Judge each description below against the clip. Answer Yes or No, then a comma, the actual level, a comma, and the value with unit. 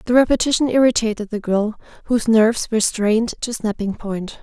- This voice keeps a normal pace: Yes, average, 165 wpm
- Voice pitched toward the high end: Yes, high, 225 Hz